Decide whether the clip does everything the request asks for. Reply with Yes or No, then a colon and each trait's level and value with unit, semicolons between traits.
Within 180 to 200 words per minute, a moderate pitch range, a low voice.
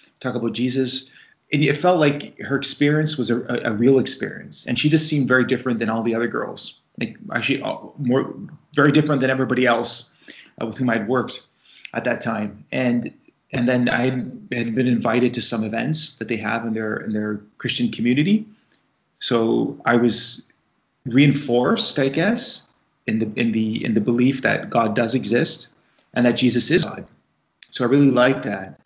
Yes: average, 185 wpm; average, 3.0 semitones; low, 125 Hz